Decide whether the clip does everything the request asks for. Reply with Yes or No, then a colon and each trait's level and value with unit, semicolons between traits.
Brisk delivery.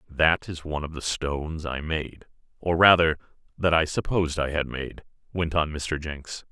No: average, 175 wpm